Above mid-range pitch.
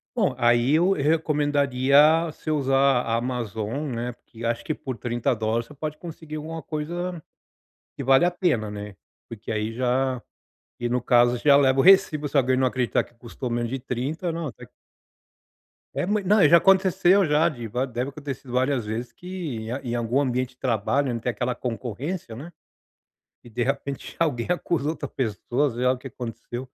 No: low, 130 Hz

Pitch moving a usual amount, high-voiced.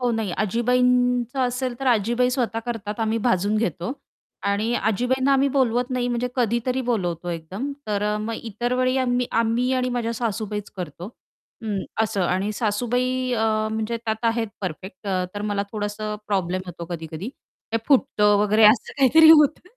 Yes: average, 3.3 semitones; high, 225 Hz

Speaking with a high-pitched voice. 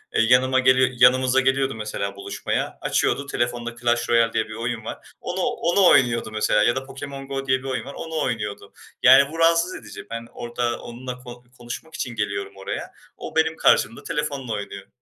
No: low, 125 Hz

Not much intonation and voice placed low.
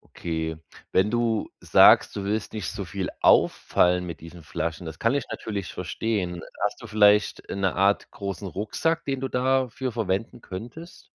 No: average, 4.4 semitones; low, 100 Hz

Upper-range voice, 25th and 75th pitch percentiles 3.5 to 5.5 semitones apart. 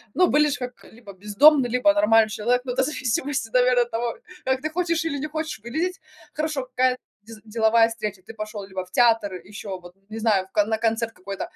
Yes: high, 230 Hz; average, 4.1 semitones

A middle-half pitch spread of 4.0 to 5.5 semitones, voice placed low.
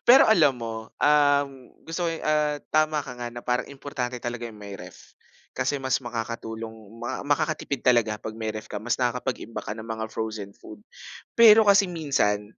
Yes: average, 4.9 semitones; low, 125 Hz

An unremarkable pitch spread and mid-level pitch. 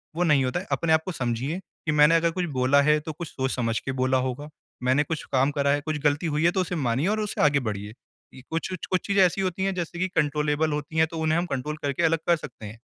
Yes: average, 4.0 semitones; medium, 150 Hz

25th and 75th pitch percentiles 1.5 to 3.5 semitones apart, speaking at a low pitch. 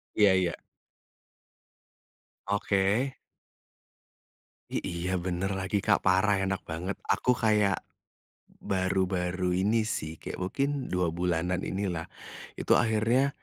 Yes: average, 2.8 semitones; very low, 95 Hz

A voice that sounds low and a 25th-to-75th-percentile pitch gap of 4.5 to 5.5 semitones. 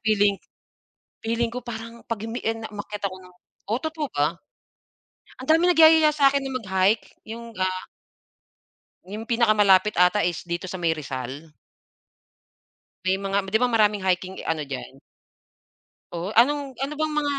No: high, 215 Hz; average, 5.1 semitones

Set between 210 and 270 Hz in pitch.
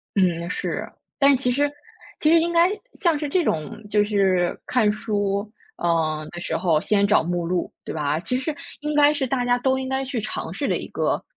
Yes: high, 215 Hz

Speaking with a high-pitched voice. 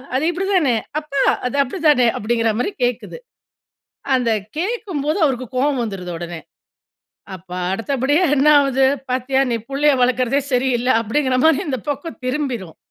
Yes: very high, 260 Hz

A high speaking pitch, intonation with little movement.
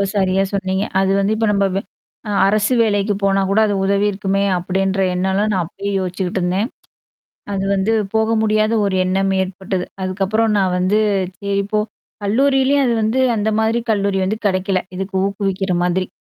Yes: high, 195 Hz; narrow, 2.0 semitones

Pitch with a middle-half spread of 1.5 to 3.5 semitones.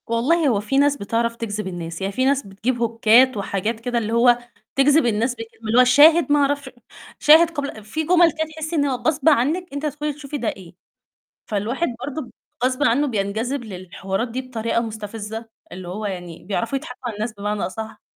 No: average, 5.1 semitones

